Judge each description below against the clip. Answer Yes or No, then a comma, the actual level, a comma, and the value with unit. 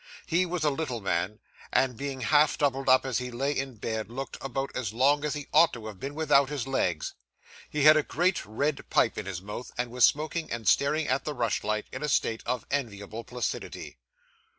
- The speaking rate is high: Yes, fast, 215 wpm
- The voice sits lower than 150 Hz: Yes, low, 135 Hz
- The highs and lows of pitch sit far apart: No, average, 4.3 semitones